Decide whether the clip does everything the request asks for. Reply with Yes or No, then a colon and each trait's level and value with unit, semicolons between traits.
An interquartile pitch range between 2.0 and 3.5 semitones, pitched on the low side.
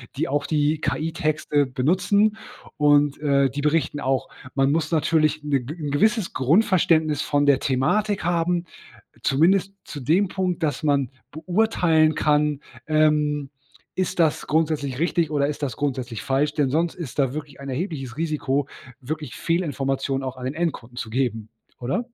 No: average, 3.2 semitones; medium, 150 Hz